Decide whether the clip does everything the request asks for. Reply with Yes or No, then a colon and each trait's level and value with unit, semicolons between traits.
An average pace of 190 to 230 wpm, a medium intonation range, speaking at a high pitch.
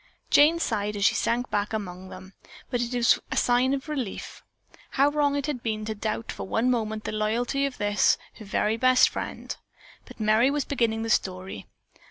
Yes: average, 195 wpm; average, 3.4 semitones; high, 225 Hz